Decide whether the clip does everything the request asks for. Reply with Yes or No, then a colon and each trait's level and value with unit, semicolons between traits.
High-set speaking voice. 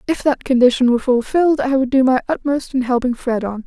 Yes: very high, 260 Hz